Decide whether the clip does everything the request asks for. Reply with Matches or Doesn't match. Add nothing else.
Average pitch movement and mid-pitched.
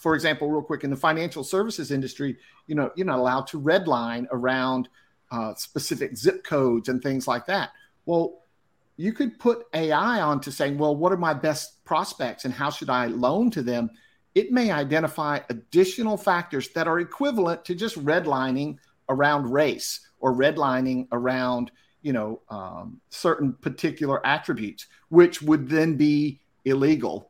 Matches